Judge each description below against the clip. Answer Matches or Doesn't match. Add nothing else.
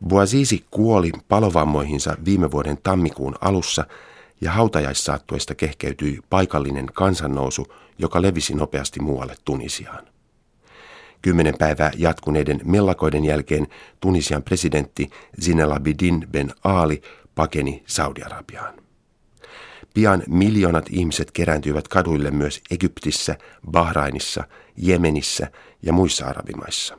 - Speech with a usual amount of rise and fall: Matches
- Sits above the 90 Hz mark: Doesn't match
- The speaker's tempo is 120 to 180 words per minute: Doesn't match